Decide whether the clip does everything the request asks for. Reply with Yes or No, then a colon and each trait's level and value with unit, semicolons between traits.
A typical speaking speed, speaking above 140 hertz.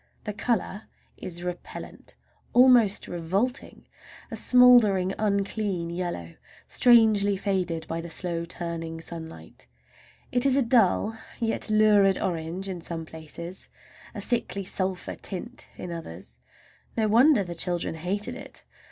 No: slow, 125 wpm; high, 190 Hz